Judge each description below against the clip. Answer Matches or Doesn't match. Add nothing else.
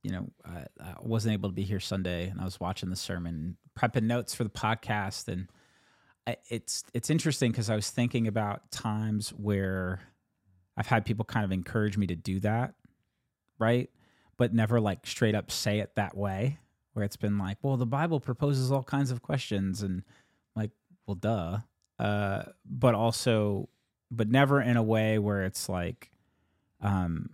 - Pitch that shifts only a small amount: Doesn't match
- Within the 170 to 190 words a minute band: Matches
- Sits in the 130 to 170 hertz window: Doesn't match